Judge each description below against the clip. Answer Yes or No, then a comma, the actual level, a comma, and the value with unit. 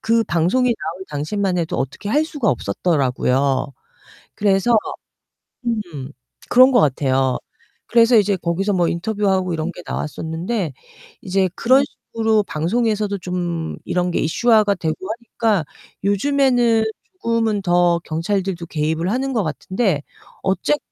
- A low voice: No, high, 190 Hz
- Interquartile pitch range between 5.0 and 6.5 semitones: Yes, wide, 5.4 semitones